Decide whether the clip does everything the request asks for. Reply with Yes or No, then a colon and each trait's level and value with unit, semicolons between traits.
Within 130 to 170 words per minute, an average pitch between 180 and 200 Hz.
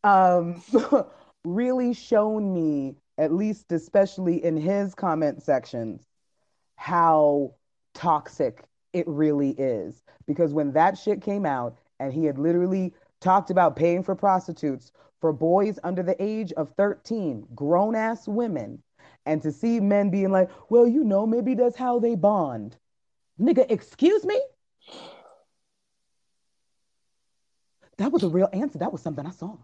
Yes: average, 140 wpm; medium, 185 Hz